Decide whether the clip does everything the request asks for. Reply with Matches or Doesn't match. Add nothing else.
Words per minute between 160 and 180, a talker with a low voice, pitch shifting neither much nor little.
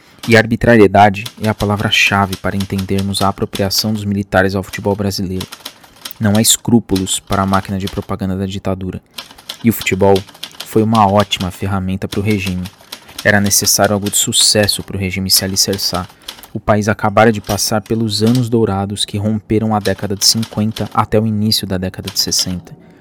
Doesn't match